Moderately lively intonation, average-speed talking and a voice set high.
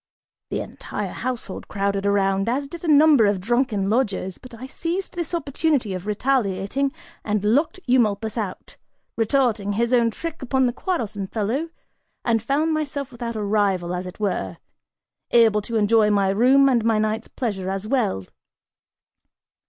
Yes: average, 4.9 semitones; average, 155 wpm; high, 225 Hz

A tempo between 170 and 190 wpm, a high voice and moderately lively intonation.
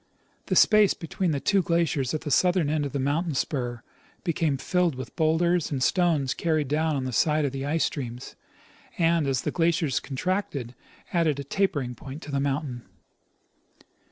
No: average, 175 wpm; medium, 150 Hz; average, 3.8 semitones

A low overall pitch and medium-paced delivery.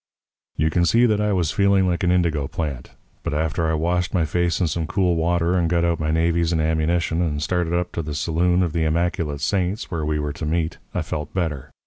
No: very low, 85 Hz; fast, 235 wpm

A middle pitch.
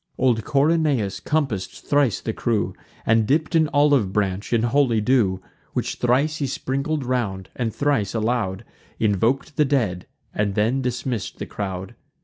No: low, 120 Hz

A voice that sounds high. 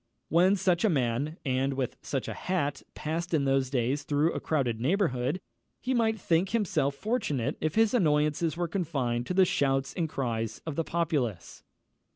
No: medium, 150 Hz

